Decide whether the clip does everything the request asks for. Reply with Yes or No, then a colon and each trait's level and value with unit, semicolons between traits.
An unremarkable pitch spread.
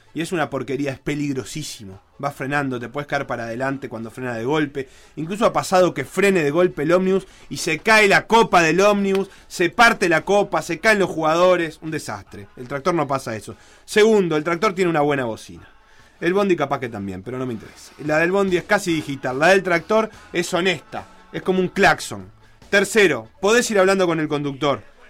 No: wide, 5.8 semitones